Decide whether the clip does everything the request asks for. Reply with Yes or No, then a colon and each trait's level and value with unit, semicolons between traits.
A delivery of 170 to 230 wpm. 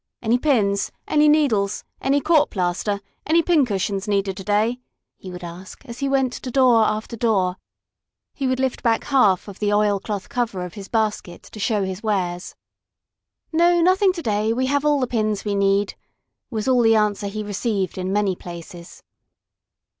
Yes: average, 175 wpm